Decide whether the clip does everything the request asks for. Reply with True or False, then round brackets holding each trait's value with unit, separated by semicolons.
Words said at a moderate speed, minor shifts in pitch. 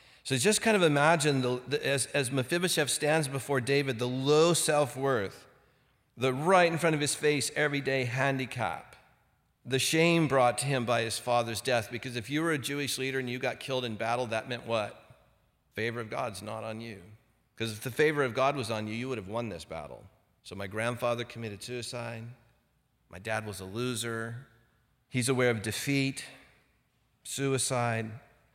False (185 wpm; 3.4 semitones)